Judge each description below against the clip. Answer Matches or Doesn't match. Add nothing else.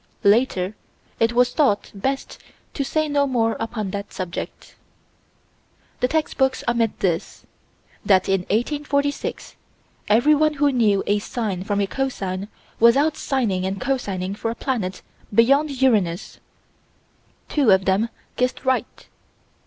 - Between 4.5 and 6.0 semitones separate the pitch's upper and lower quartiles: Matches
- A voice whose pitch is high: Matches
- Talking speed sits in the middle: Doesn't match